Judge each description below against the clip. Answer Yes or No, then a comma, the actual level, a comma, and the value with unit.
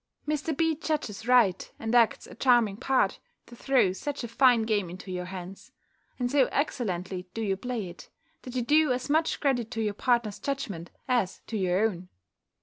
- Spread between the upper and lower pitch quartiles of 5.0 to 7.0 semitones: Yes, average, 5.3 semitones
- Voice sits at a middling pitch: No, high, 230 Hz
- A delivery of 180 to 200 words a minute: Yes, average, 185 wpm